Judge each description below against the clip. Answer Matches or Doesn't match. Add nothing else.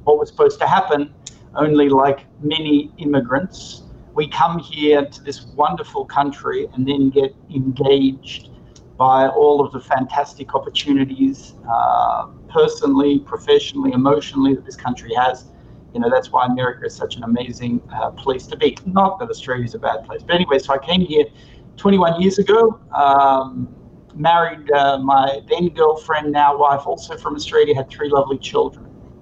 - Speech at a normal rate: Matches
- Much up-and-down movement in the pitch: Matches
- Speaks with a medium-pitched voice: Matches